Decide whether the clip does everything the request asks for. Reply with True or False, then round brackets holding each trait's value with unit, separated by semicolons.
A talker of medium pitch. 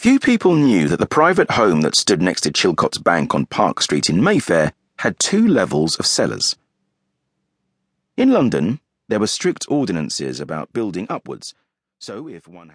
False (205 Hz)